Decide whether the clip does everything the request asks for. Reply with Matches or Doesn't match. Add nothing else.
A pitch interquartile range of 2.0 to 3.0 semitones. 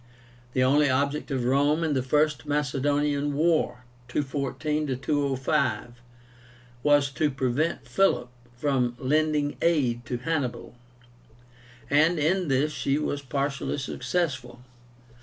Matches